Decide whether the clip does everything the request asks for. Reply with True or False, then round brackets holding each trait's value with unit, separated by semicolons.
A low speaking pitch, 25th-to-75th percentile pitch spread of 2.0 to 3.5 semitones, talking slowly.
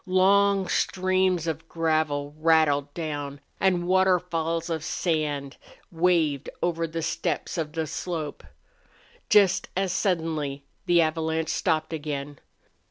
False (165 Hz; 2.7 semitones; 110 wpm)